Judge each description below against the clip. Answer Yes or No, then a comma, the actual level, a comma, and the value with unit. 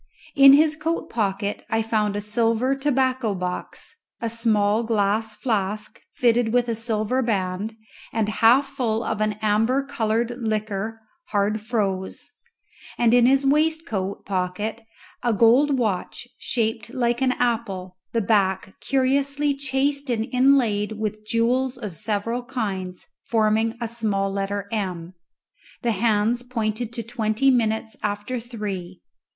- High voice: Yes, high, 225 Hz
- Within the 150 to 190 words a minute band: No, slow, 135 wpm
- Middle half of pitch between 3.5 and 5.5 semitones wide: No, average, 3.1 semitones